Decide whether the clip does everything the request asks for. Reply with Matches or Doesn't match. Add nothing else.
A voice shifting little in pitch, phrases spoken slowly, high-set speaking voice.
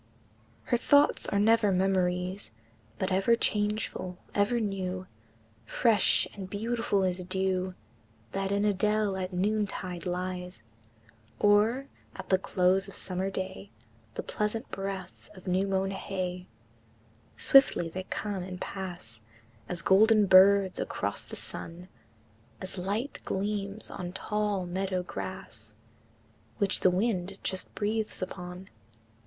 Matches